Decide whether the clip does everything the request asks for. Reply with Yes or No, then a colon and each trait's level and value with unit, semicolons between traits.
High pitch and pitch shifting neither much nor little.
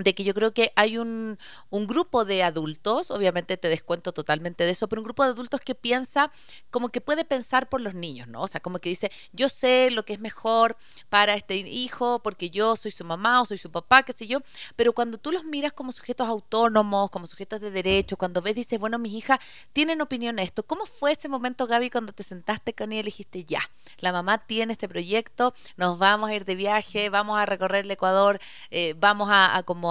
Yes: high, 215 Hz; average, 4.2 semitones